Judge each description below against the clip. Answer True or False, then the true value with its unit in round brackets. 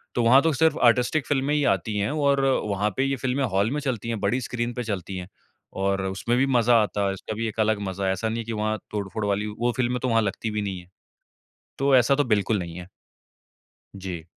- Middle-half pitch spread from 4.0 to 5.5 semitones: True (4.3 semitones)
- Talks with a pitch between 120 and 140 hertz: False (110 Hz)